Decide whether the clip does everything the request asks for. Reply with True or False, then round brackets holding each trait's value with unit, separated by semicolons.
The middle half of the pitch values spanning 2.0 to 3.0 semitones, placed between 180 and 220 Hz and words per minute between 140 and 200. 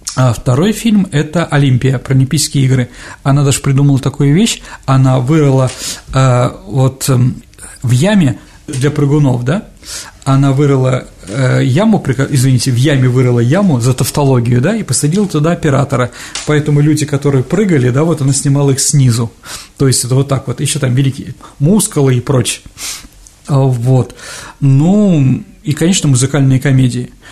False (2.5 semitones; 135 Hz; 145 wpm)